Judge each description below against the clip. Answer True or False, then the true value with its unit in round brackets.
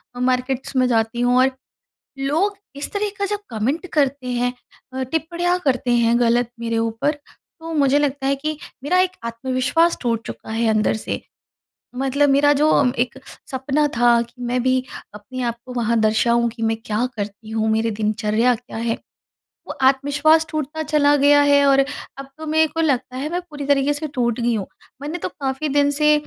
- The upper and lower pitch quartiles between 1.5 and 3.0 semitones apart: False (3.7 semitones)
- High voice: True (260 Hz)